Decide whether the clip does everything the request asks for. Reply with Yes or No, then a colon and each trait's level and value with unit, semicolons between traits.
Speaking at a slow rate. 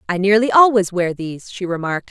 No: average, 200 wpm